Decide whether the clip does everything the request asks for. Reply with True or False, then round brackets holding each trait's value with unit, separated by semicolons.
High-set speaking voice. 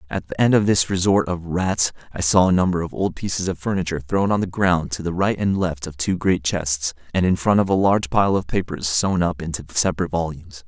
False (90 Hz)